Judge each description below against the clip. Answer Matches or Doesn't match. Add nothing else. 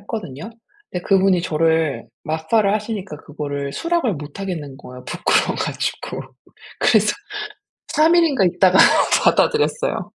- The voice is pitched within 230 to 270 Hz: Doesn't match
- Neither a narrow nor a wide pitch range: Doesn't match